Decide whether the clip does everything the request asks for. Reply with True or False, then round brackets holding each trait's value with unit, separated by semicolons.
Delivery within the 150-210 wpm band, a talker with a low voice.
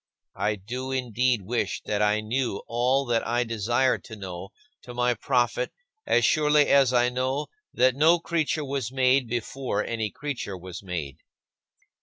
True (155 wpm; 120 Hz)